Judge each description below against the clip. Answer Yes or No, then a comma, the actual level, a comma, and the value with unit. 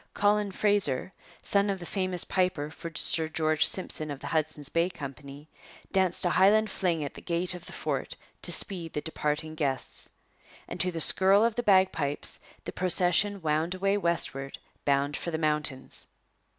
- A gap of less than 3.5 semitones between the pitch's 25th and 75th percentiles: No, average, 3.9 semitones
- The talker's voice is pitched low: No, medium, 170 Hz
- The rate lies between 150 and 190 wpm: Yes, average, 170 wpm